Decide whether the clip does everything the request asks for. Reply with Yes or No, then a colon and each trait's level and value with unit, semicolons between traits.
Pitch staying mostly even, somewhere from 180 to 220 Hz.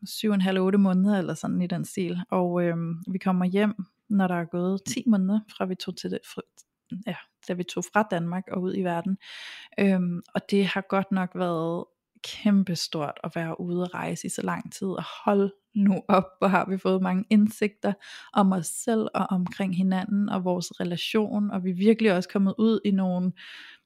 Yes: narrow, 2.1 semitones; high, 190 Hz